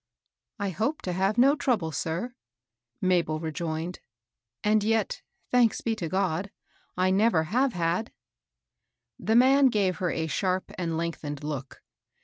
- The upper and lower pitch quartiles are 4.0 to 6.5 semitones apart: Yes, average, 5.3 semitones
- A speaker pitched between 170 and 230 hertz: Yes, medium, 185 Hz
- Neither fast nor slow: Yes, average, 160 wpm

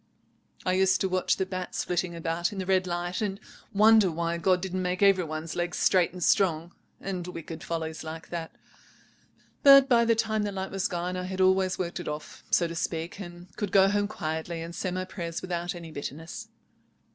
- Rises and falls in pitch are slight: Yes, narrow, 2.1 semitones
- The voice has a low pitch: No, medium, 180 Hz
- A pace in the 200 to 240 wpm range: Yes, fast, 205 wpm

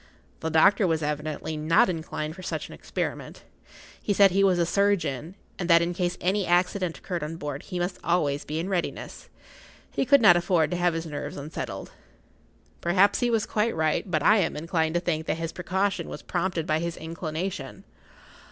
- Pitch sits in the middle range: Yes, medium, 175 Hz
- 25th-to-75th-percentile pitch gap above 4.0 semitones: No, average, 2.9 semitones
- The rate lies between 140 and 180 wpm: No, average, 190 wpm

